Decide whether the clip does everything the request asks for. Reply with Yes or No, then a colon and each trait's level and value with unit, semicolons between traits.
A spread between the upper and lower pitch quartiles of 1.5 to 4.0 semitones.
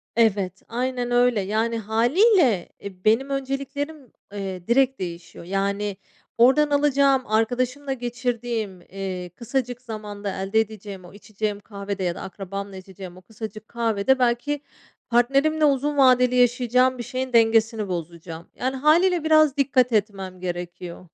No: average, 4.7 semitones